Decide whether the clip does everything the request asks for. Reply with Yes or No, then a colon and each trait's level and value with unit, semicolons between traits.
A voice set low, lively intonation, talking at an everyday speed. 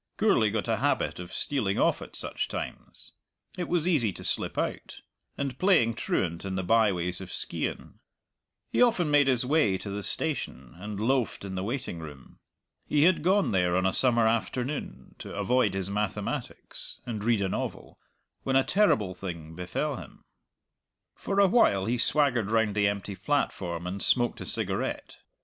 Yes: low, 110 Hz; wide, 6.7 semitones; average, 170 wpm